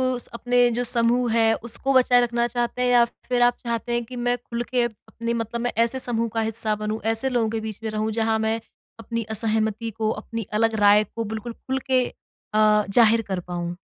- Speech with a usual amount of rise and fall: No, narrow, 1.6 semitones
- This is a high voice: Yes, high, 230 Hz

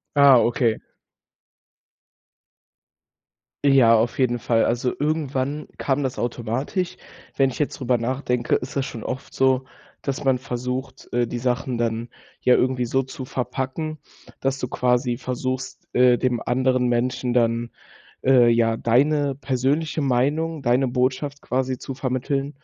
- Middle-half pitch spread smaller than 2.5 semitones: Yes, narrow, 2.0 semitones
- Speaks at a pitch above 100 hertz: Yes, low, 130 Hz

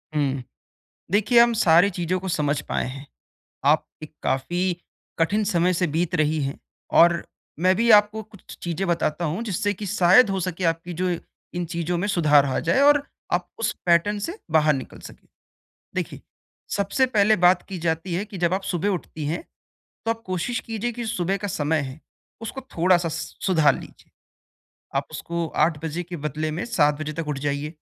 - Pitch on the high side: No, medium, 175 Hz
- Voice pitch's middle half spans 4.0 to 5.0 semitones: Yes, average, 4.3 semitones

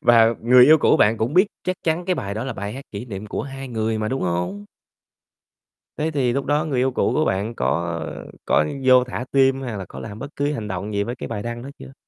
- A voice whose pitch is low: Yes, low, 120 Hz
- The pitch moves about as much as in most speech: Yes, average, 4.5 semitones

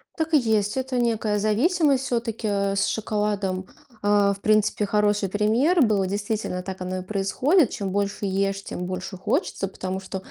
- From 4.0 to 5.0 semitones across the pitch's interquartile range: No, average, 2.8 semitones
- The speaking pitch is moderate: No, high, 205 Hz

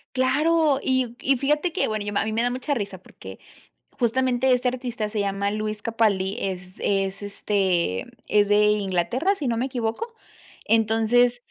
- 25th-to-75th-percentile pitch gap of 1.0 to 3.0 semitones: No, average, 4.1 semitones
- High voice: Yes, high, 225 Hz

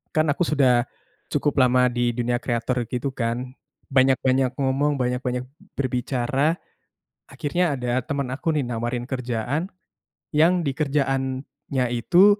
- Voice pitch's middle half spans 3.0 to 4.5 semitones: No, narrow, 2.6 semitones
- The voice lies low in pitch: Yes, low, 130 Hz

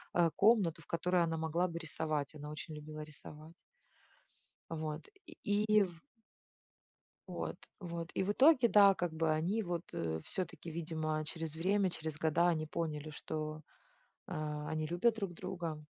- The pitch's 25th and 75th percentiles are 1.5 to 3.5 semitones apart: Yes, average, 2.8 semitones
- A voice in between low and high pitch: Yes, medium, 165 Hz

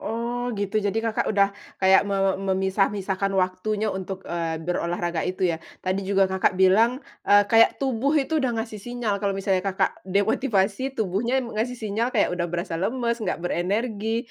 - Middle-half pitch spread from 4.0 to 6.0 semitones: No, average, 3.4 semitones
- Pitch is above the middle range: Yes, high, 200 Hz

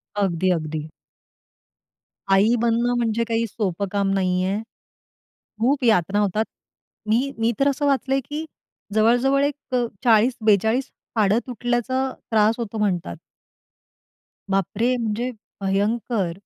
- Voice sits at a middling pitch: No, high, 225 Hz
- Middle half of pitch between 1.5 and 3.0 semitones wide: No, average, 3.7 semitones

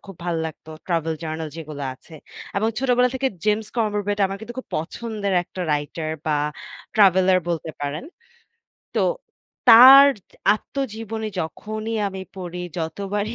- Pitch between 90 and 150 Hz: No, high, 200 Hz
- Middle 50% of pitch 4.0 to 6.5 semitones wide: Yes, average, 5.3 semitones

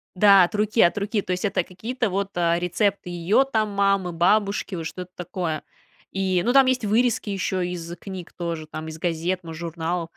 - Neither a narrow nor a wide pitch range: Yes, average, 3.0 semitones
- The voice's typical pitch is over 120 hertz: Yes, medium, 185 Hz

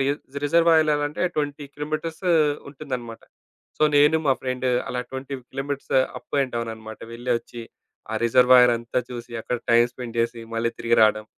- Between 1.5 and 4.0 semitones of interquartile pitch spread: Yes, average, 3.6 semitones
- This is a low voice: Yes, low, 125 Hz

